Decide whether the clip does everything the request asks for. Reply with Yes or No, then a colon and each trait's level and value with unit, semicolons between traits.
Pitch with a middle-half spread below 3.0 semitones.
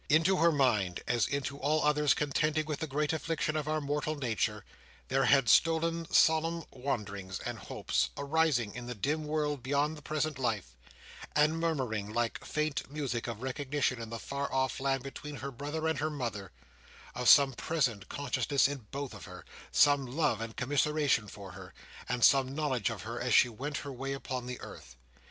No: average, 3.7 semitones